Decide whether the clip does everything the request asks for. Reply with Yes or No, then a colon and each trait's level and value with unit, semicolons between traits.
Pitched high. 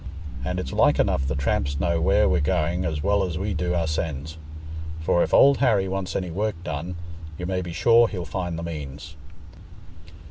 No: very low, 85 Hz